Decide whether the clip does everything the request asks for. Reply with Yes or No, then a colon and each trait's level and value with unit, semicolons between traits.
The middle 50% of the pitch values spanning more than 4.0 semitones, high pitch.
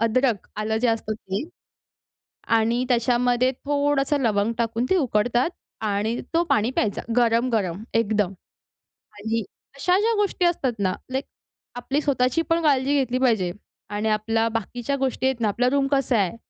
No: average, 3.5 semitones; high, 240 Hz